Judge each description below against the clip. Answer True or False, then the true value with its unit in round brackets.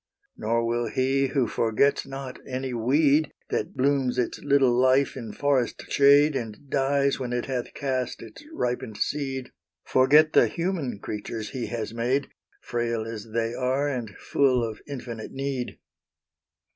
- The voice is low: True (130 Hz)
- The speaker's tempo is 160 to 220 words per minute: False (145 wpm)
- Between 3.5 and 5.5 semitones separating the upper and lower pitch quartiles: False (2.9 semitones)